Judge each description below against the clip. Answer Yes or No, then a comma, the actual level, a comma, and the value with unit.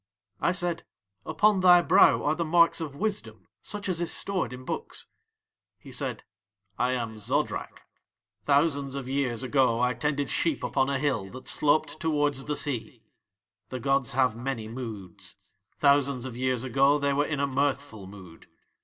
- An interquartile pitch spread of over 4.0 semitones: No, average, 3.2 semitones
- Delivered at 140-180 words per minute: Yes, average, 160 wpm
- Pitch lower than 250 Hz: Yes, medium, 140 Hz